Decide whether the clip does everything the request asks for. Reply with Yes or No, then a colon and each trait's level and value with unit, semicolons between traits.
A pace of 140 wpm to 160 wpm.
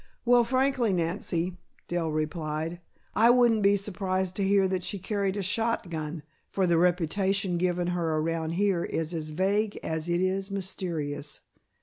Yes: average, 150 wpm